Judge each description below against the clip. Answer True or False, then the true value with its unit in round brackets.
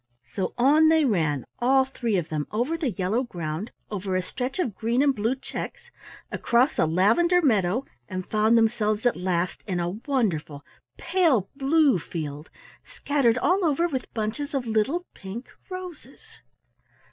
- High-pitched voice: True (235 Hz)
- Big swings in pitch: True (7.0 semitones)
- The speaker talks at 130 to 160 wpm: True (155 wpm)